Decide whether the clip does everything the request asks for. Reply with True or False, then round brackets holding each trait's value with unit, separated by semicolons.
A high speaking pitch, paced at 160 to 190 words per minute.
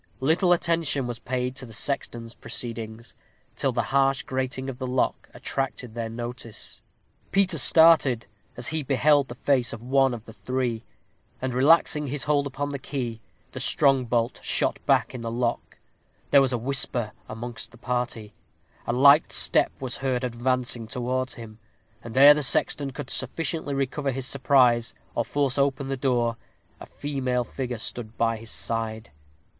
False (130 Hz; 165 wpm)